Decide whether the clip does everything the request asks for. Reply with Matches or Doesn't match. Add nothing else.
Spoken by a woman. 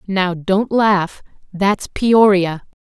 Matches